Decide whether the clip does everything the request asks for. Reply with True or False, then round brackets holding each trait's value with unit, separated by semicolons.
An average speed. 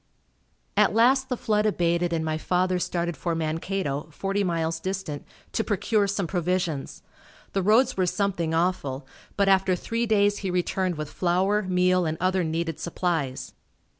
True (155 wpm)